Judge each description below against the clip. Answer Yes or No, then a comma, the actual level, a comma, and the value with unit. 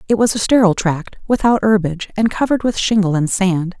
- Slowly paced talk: No, fast, 205 wpm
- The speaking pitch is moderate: No, high, 200 Hz